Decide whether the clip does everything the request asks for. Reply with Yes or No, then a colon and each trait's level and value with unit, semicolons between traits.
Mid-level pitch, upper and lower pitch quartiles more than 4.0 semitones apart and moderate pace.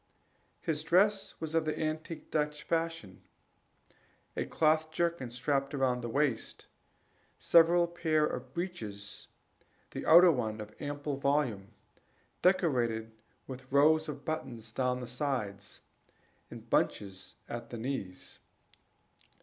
No: medium, 145 Hz; average, 5.0 semitones; slow, 115 wpm